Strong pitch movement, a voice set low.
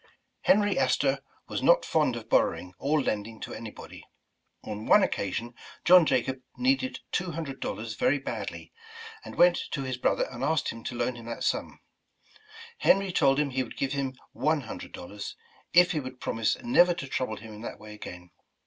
Yes: wide, 6.0 semitones; low, 130 Hz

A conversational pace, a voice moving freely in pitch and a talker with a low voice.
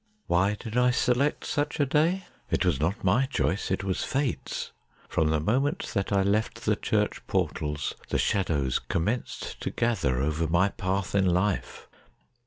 Yes: average, 165 wpm; wide, 6.4 semitones; low, 100 Hz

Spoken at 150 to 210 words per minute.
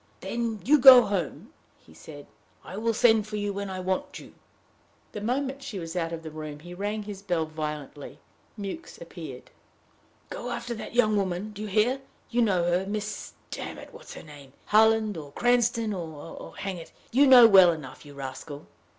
Yes: average, 190 wpm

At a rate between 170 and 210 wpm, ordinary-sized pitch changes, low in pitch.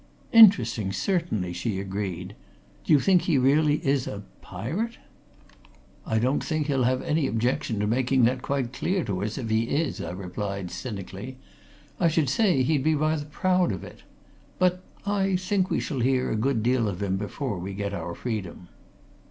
No: average, 175 wpm; wide, 7.2 semitones; low, 130 Hz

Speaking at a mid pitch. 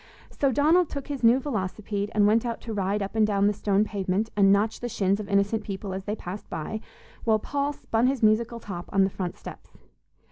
No: high, 210 Hz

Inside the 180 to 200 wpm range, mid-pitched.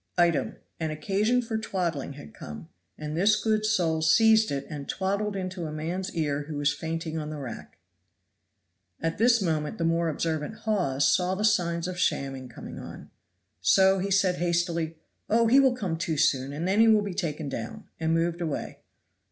Yes: average, 185 wpm; medium, 170 Hz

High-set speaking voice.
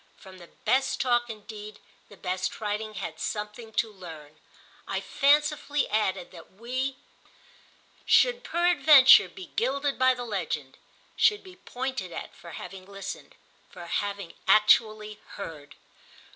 Yes: high, 215 Hz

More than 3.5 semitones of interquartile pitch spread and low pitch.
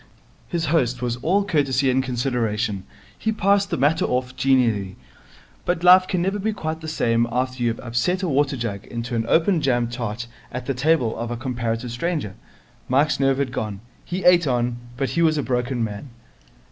Yes: average, 5.2 semitones; low, 130 Hz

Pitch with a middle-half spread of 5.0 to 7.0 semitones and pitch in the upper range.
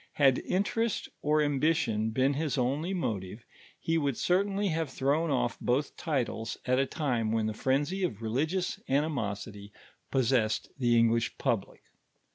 No: wide, 5.5 semitones; low, 135 Hz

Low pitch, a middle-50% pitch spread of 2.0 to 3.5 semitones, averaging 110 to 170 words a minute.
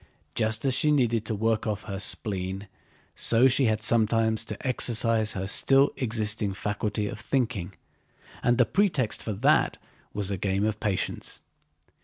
Yes: low, 110 Hz; narrow, 2.6 semitones; average, 150 wpm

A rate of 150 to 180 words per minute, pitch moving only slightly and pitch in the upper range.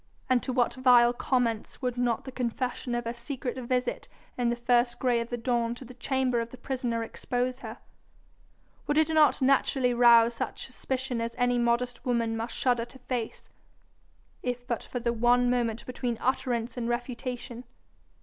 Yes: average, 175 wpm; narrow, 1.2 semitones; high, 245 Hz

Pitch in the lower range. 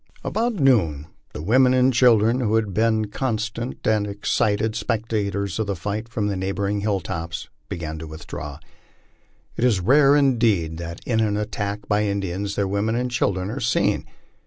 Yes: low, 105 Hz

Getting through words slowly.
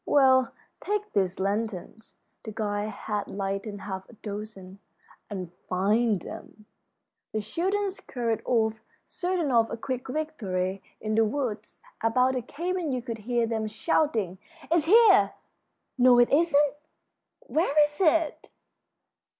Yes: slow, 130 wpm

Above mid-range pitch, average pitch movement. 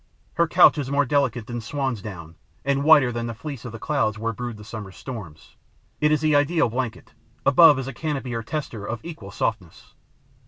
No: low, 125 Hz; average, 4.6 semitones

